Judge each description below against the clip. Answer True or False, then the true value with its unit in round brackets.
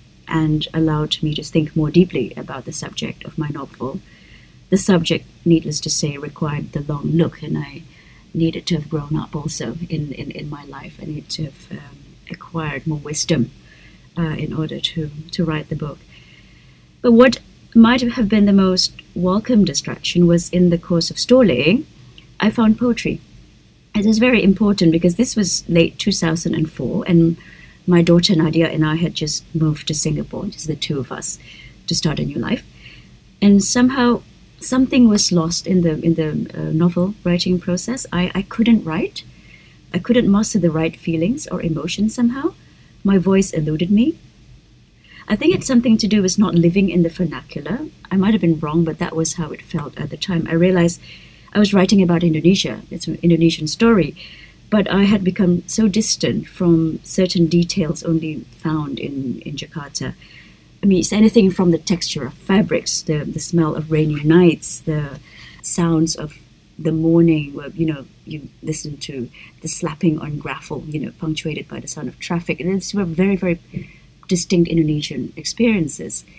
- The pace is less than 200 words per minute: True (180 wpm)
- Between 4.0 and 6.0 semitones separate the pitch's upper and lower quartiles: False (3.5 semitones)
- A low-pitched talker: False (170 Hz)